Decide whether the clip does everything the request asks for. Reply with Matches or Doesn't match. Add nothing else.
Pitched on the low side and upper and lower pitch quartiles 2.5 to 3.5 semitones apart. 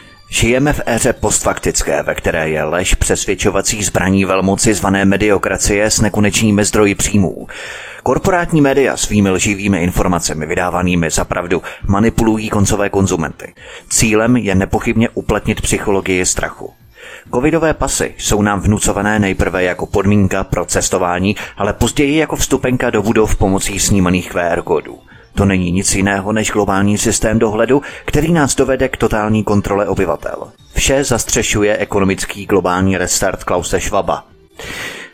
Matches